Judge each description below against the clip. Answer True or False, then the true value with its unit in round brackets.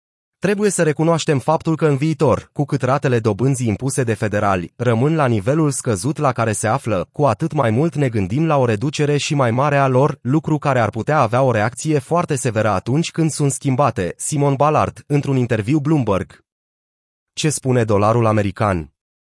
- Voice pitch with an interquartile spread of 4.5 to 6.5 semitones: True (4.9 semitones)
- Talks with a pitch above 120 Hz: True (135 Hz)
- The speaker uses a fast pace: True (180 wpm)